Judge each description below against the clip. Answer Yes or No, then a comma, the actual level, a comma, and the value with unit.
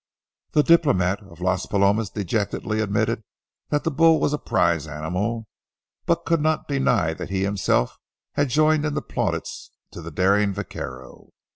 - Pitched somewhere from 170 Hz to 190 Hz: No, low, 105 Hz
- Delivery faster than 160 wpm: No, average, 155 wpm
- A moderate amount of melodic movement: No, wide, 8.0 semitones